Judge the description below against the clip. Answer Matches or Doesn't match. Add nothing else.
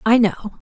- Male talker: Doesn't match